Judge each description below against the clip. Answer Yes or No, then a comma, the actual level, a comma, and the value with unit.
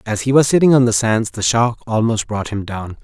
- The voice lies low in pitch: Yes, low, 115 Hz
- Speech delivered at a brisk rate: Yes, fast, 255 wpm